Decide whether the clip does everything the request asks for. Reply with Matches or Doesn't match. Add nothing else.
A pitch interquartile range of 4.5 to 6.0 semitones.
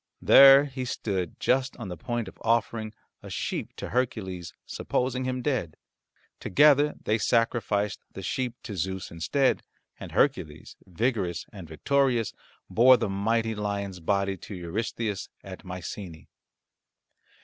Matches